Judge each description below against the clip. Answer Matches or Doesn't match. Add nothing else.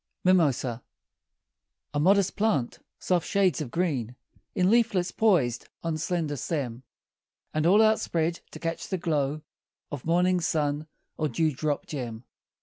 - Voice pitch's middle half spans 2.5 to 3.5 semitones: Doesn't match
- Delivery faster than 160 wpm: Doesn't match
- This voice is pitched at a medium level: Matches